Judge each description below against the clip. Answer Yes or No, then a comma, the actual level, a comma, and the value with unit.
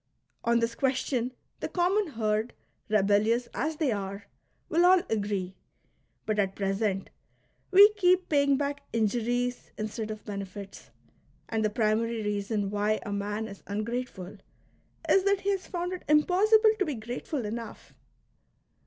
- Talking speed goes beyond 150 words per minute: No, average, 140 wpm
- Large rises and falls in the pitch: Yes, wide, 6.4 semitones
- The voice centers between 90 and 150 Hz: No, high, 230 Hz